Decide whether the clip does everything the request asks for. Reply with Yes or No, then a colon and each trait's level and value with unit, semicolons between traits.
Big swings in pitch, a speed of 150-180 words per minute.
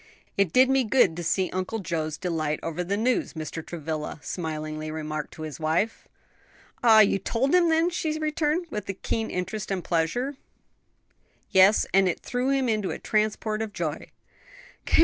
Yes: wide, 7.2 semitones; average, 170 wpm